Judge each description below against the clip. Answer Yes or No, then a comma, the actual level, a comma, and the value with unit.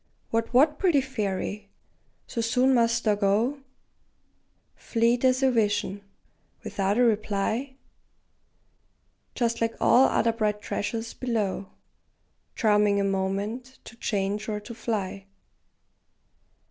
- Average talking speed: No, slow, 110 wpm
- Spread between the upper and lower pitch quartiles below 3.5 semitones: Yes, average, 3.1 semitones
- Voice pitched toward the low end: No, high, 225 Hz